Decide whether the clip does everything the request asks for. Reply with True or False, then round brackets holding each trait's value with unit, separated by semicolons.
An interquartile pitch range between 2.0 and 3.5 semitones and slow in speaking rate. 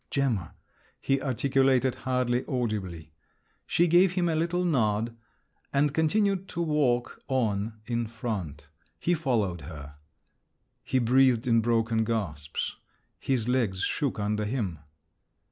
False (4.5 semitones; 120 wpm)